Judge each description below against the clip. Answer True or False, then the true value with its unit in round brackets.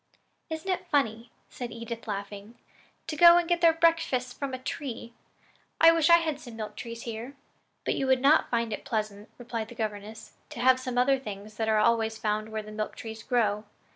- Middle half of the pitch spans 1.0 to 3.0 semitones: False (4.1 semitones)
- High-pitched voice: True (235 Hz)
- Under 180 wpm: False (200 wpm)